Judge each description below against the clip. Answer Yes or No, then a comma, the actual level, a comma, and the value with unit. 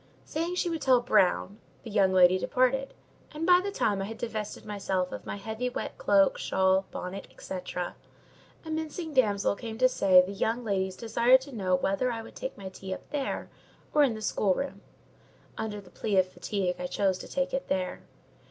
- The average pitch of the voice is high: Yes, high, 215 Hz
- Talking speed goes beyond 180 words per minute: Yes, average, 195 wpm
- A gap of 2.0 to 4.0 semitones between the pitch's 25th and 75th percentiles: No, average, 5.3 semitones